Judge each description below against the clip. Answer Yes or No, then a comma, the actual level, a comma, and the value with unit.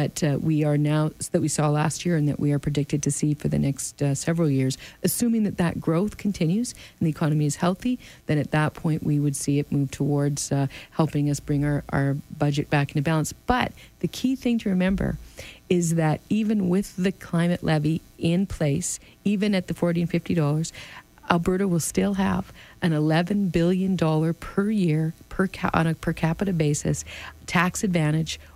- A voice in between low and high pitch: Yes, medium, 160 Hz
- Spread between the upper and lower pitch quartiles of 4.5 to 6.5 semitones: No, average, 3.8 semitones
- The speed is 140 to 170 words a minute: No, average, 200 wpm